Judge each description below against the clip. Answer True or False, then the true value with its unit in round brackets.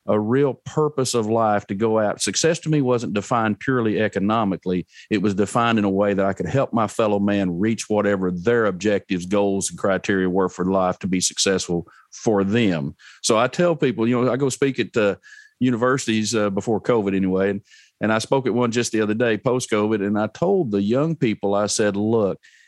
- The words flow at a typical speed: False (215 wpm)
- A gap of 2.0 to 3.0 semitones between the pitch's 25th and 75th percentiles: False (3.5 semitones)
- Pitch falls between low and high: False (110 Hz)